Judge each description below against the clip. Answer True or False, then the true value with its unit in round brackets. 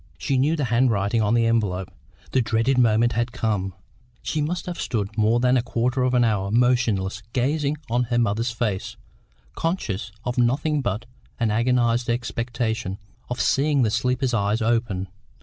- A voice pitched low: True (120 Hz)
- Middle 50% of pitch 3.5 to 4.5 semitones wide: False (2.5 semitones)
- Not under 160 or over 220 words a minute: True (165 wpm)